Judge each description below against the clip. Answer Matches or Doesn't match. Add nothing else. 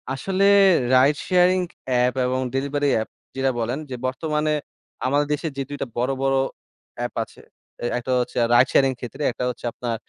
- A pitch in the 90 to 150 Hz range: Matches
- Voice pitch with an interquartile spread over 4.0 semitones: Doesn't match